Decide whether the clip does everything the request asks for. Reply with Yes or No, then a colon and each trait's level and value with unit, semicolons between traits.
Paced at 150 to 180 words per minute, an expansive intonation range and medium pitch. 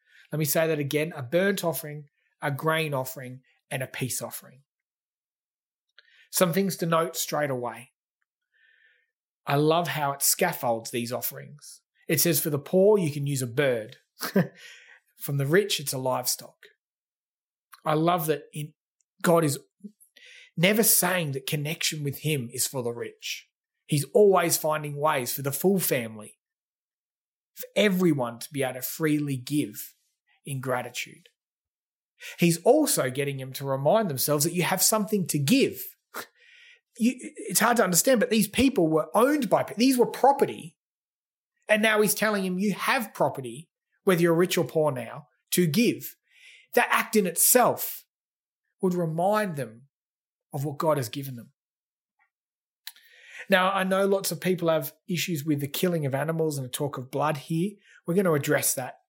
Yes: average, 160 wpm; wide, 5.8 semitones; medium, 160 Hz